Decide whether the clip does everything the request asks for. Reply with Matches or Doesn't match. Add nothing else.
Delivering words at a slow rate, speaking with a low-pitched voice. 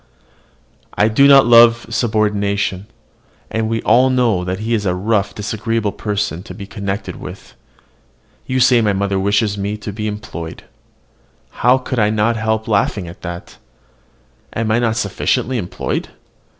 Doesn't match